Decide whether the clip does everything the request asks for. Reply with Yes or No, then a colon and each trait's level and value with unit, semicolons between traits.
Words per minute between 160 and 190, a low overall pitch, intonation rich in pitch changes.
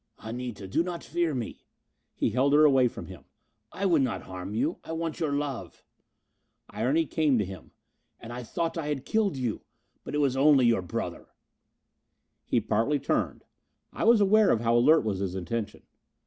Yes: average, 180 wpm; low, 130 Hz; wide, 5.9 semitones